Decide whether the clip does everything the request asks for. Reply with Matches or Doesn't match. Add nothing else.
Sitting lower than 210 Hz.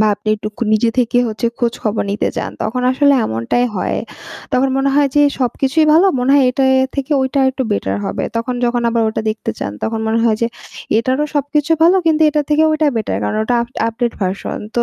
Doesn't match